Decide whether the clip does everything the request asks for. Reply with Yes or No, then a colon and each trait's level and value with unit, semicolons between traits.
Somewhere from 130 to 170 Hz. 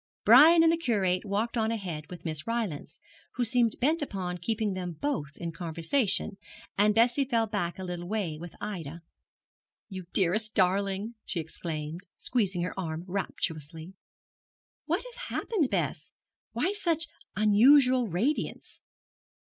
No: high, 200 Hz